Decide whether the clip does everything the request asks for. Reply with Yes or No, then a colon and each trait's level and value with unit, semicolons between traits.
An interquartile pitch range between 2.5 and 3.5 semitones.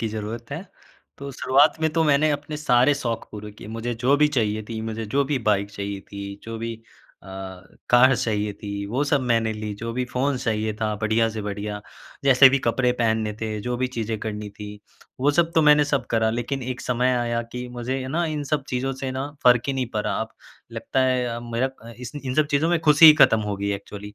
No: average, 3.9 semitones